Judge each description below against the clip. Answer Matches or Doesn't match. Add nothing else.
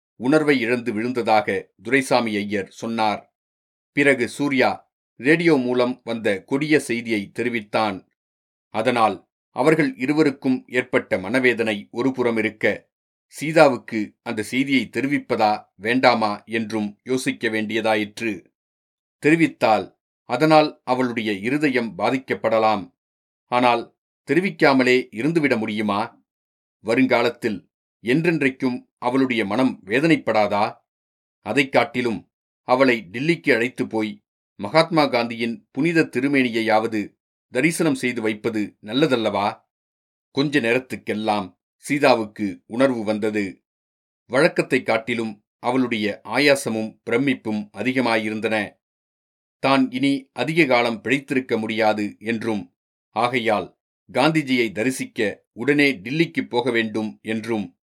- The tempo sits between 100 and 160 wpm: Doesn't match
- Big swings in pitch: Doesn't match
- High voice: Doesn't match